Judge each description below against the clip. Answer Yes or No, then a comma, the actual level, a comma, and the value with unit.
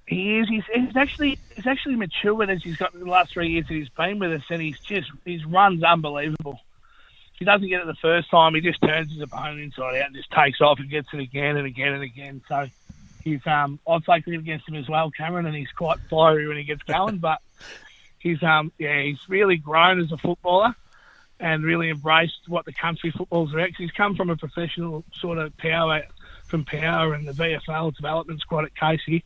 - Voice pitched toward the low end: No, medium, 160 Hz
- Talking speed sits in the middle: No, fast, 220 wpm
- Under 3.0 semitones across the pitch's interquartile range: Yes, narrow, 2.4 semitones